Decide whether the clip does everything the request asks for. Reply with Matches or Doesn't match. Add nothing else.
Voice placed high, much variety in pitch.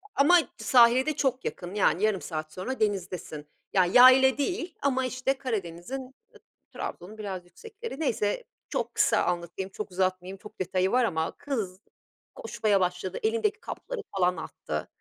Matches